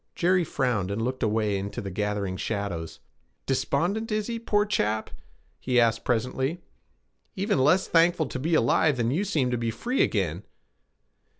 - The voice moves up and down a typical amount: No, wide, 8.6 semitones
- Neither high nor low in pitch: No, low, 125 Hz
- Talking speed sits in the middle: Yes, average, 160 wpm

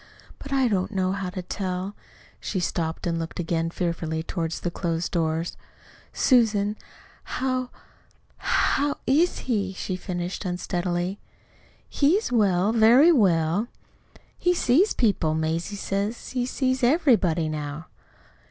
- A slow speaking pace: Yes, slow, 125 wpm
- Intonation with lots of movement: Yes, wide, 6.2 semitones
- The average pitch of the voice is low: No, high, 190 Hz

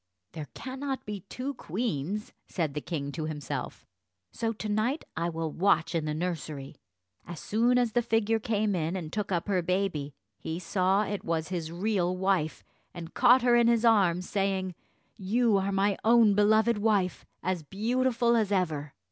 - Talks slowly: No, average, 175 wpm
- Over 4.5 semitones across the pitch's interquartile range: Yes, average, 5.0 semitones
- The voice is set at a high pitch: Yes, high, 195 Hz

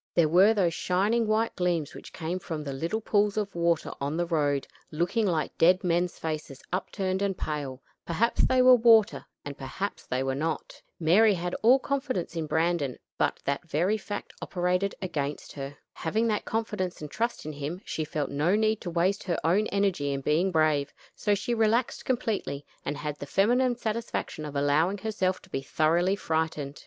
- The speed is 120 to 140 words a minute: No, average, 185 wpm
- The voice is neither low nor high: Yes, medium, 175 Hz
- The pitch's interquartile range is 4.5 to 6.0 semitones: Yes, wide, 5.4 semitones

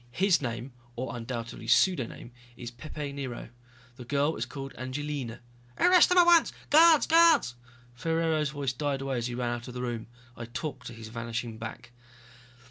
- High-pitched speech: No, low, 130 Hz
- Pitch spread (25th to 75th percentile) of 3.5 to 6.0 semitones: Yes, average, 4.1 semitones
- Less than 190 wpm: Yes, average, 175 wpm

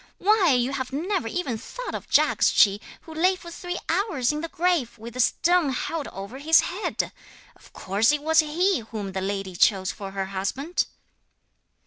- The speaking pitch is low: No, very high, 280 Hz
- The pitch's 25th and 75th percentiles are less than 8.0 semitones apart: No, wide, 8.4 semitones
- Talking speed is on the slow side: No, average, 175 wpm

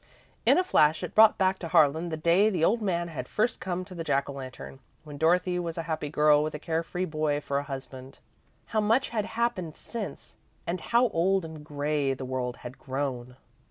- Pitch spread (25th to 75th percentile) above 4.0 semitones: Yes, average, 4.5 semitones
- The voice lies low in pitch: No, medium, 160 Hz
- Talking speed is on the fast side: Yes, fast, 215 wpm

